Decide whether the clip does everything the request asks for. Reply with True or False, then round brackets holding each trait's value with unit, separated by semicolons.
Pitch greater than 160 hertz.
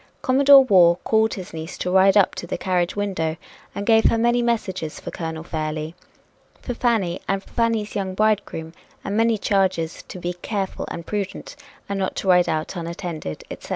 True (190 Hz)